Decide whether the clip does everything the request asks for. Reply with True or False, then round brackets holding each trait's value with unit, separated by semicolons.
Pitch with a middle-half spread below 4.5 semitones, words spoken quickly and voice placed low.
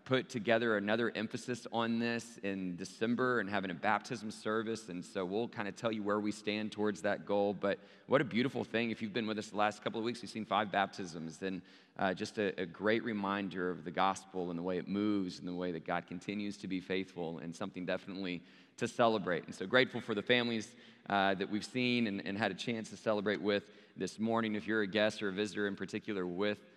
True (2.8 semitones; 235 wpm; 105 Hz)